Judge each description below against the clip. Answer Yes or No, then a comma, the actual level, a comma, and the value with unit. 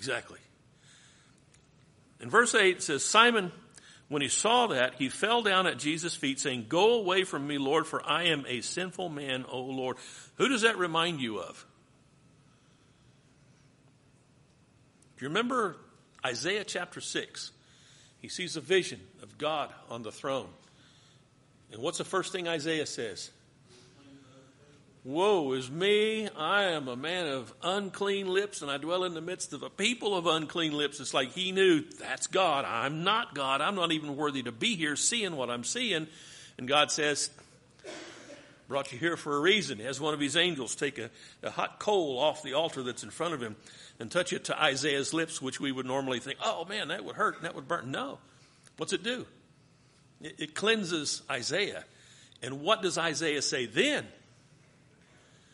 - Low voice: No, medium, 145 Hz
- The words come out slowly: No, average, 175 wpm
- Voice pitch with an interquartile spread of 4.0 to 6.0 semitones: Yes, average, 4.7 semitones